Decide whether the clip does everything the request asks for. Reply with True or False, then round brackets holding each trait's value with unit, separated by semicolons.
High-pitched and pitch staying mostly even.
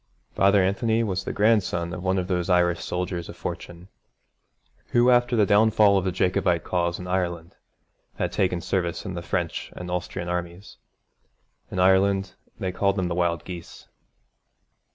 False (90 Hz; 2.1 semitones)